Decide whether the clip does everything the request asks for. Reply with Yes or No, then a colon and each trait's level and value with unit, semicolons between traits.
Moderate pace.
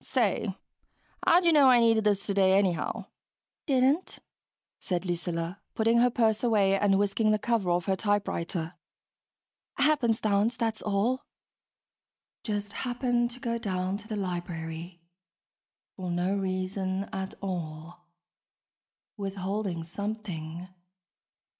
No: slow, 115 wpm